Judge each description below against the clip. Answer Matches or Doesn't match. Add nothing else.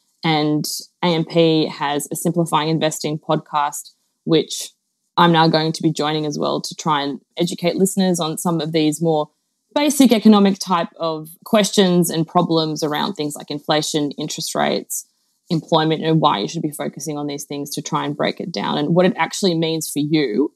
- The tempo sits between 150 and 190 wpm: Matches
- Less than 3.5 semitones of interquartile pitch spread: Matches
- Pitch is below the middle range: Doesn't match